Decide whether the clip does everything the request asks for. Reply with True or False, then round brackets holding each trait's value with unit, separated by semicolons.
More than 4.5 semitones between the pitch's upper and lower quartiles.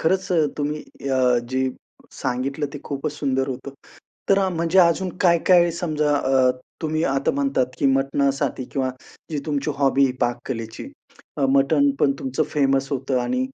False (2.9 semitones)